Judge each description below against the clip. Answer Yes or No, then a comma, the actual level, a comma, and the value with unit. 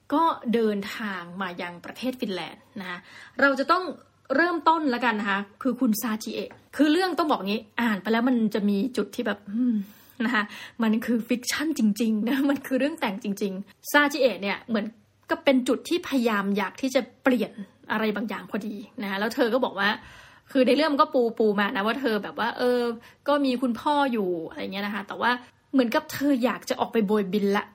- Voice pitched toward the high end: Yes, high, 235 Hz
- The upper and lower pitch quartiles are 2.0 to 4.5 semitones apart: Yes, average, 4.2 semitones